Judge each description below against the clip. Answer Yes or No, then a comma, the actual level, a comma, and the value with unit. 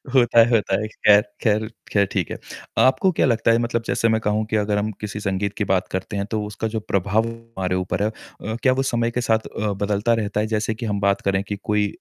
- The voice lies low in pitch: Yes, low, 105 Hz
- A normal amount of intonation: No, narrow, 2.0 semitones